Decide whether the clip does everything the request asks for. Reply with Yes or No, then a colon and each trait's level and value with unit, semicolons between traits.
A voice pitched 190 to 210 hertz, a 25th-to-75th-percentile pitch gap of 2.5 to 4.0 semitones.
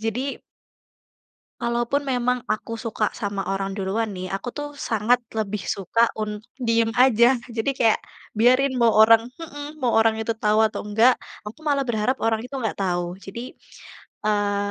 No: high, 225 Hz; average, 2.9 semitones